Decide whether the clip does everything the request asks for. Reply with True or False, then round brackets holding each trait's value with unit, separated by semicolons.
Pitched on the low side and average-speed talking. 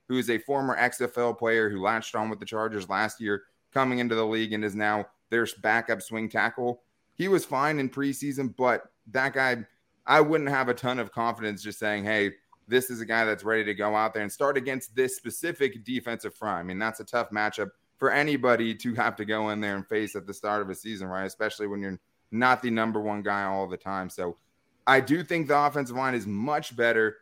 False (115 Hz; 230 wpm)